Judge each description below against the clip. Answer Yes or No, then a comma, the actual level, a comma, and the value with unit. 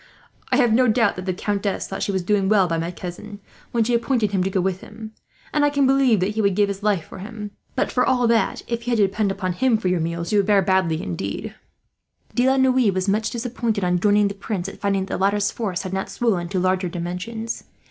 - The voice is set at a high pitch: Yes, high, 200 Hz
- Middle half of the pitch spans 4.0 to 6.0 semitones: No, average, 3.5 semitones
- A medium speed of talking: No, fast, 255 wpm